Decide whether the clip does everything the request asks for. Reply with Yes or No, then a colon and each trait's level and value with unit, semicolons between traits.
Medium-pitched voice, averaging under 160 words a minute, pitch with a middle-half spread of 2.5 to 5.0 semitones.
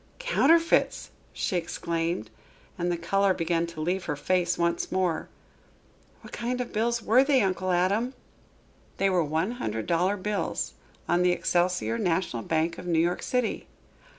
Yes: medium, 180 Hz; average, 150 wpm; average, 3.7 semitones